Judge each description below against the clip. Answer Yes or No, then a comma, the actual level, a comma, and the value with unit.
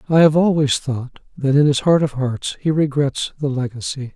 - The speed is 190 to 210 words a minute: Yes, average, 200 wpm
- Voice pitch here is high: No, medium, 140 Hz